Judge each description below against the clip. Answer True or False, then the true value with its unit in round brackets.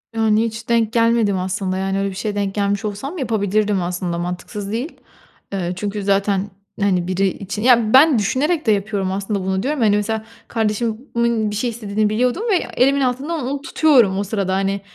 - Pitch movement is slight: False (3.2 semitones)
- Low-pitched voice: False (210 Hz)